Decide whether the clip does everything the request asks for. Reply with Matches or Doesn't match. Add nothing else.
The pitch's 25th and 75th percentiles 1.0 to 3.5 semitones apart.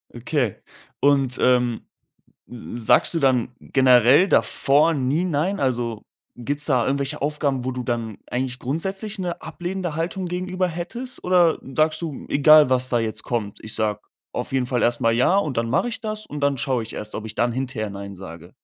Doesn't match